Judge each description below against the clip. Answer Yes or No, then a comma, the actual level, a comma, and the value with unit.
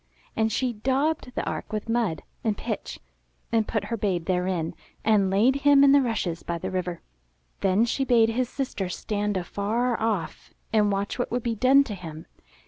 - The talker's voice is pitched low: No, high, 220 Hz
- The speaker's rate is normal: Yes, average, 185 wpm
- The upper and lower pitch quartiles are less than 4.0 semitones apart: No, average, 4.4 semitones